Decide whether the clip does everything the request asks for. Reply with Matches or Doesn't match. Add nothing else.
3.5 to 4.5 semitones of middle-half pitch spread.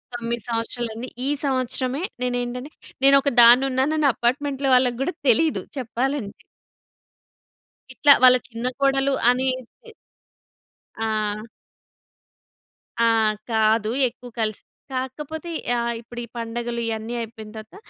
Doesn't match